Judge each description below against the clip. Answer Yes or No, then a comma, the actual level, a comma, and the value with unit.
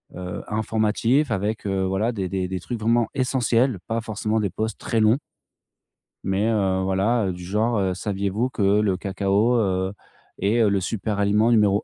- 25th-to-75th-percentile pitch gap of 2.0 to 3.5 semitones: Yes, average, 2.8 semitones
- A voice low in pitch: Yes, low, 105 Hz